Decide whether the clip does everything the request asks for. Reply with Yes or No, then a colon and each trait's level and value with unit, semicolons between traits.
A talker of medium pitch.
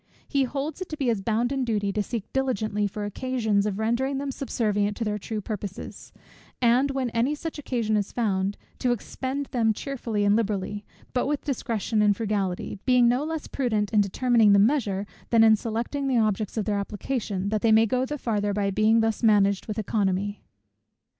No: high, 220 Hz